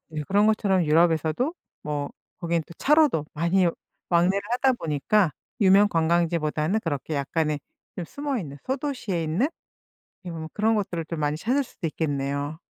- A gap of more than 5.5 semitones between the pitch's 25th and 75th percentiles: No, average, 5.2 semitones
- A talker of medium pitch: Yes, medium, 170 Hz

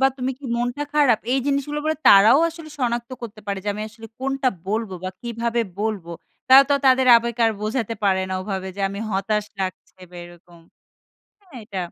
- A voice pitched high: Yes, high, 230 Hz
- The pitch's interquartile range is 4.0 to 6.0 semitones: Yes, average, 4.8 semitones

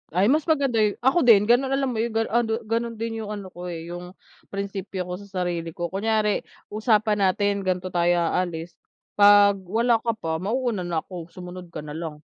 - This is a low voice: No, high, 200 Hz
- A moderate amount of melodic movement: Yes, average, 4.1 semitones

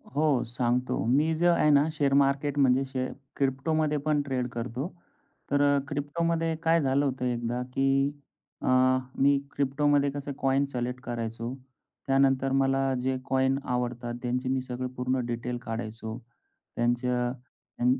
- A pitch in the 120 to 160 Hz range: Yes, low, 135 Hz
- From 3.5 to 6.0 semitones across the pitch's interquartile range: No, narrow, 2.4 semitones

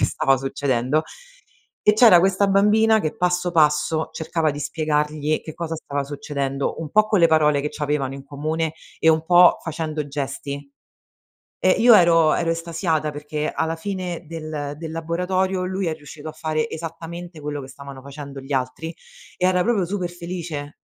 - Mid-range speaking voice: Yes, medium, 160 Hz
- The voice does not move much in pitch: No, average, 3.1 semitones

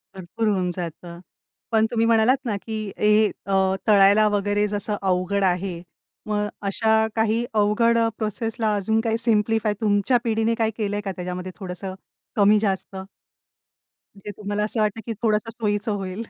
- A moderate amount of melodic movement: No, narrow, 2.1 semitones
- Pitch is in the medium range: No, high, 210 Hz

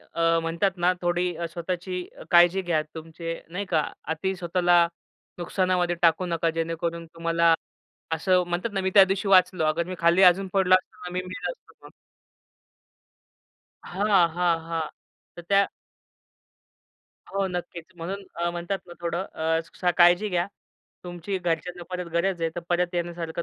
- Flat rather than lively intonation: Yes, narrow, 1.7 semitones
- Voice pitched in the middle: Yes, medium, 175 Hz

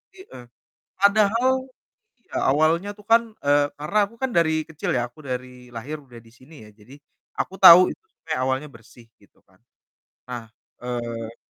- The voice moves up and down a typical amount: No, wide, 7.0 semitones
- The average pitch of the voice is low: No, medium, 145 Hz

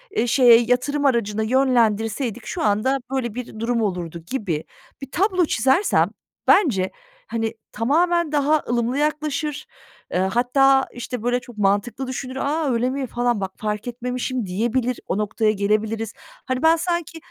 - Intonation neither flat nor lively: Yes, average, 3.9 semitones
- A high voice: Yes, high, 245 Hz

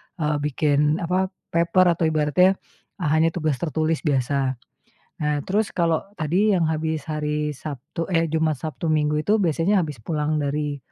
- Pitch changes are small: Yes, narrow, 2.0 semitones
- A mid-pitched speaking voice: Yes, medium, 155 Hz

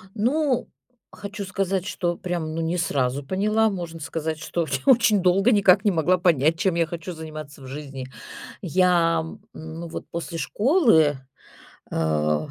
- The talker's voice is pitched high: No, medium, 170 Hz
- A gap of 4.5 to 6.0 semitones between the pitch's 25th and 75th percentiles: No, average, 3.8 semitones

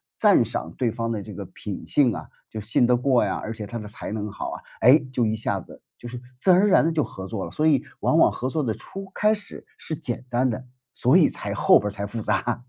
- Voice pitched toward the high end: No, low, 120 Hz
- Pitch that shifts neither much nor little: Yes, average, 4.4 semitones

